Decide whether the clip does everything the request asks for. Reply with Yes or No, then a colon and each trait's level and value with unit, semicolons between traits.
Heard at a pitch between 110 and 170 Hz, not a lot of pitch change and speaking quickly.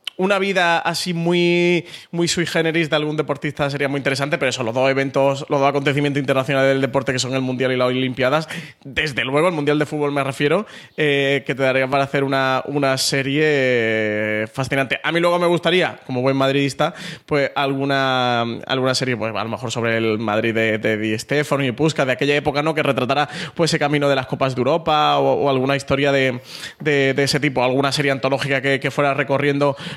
Yes: medium, 140 Hz; narrow, 2.3 semitones; fast, 205 wpm